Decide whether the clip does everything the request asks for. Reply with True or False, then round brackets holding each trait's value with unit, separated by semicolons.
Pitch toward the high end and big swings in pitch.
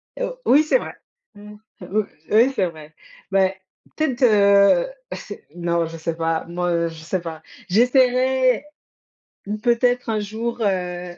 True (205 Hz; 6.2 semitones)